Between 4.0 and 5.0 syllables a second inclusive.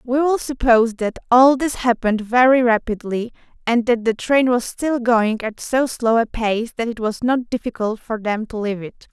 Yes: 4.9 syllables/s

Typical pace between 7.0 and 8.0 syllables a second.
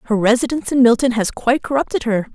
Yes: 7.1 syllables/s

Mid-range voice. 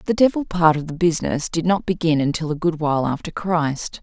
Yes: medium, 165 Hz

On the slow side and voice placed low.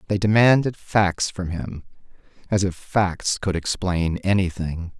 Yes: slow, 130 wpm; very low, 95 Hz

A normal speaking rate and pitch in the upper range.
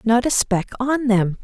No: fast, 210 wpm; high, 230 Hz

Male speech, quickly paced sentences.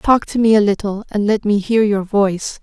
No: female; fast, 250 wpm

